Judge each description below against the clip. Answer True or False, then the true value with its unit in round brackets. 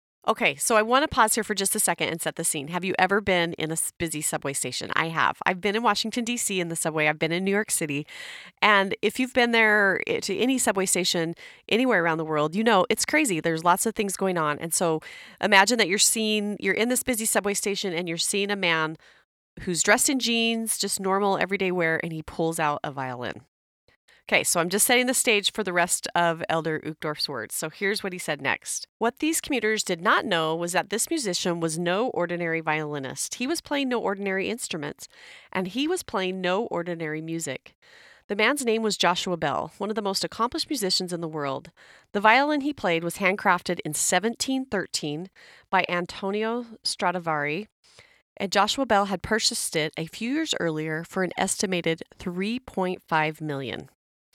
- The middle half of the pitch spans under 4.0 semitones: False (4.9 semitones)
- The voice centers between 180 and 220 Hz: True (190 Hz)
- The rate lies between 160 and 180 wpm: False (200 wpm)